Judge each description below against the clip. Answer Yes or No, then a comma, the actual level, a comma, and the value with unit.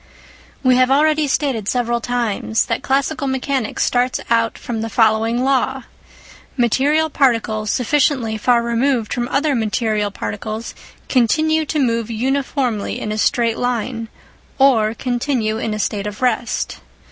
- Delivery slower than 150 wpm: Yes, slow, 135 wpm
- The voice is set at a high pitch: Yes, high, 240 Hz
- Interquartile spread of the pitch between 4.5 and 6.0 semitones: No, average, 3.3 semitones